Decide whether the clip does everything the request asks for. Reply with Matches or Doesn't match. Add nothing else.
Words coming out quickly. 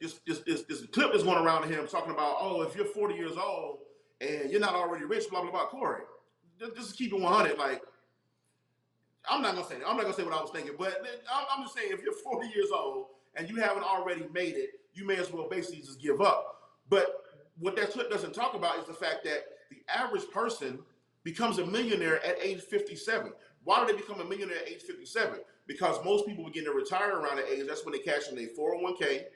Matches